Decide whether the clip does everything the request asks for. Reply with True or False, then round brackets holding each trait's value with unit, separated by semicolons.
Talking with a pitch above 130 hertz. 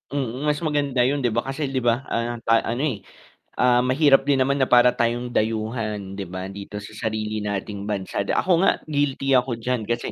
False (120 Hz)